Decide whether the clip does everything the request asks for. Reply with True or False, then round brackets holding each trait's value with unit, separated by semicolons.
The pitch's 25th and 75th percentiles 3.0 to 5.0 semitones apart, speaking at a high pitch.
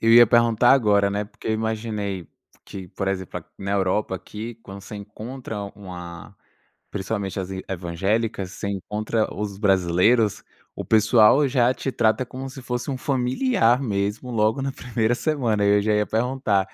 False (3.3 semitones; 110 Hz)